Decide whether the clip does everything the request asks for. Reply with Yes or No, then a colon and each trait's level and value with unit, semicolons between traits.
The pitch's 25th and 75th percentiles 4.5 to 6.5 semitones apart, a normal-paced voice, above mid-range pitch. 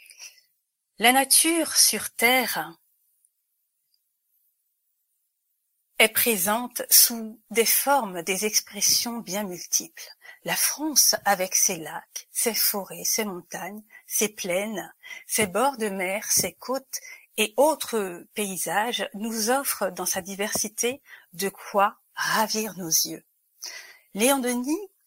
No: average, 5.0 semitones; slow, 110 wpm; high, 220 Hz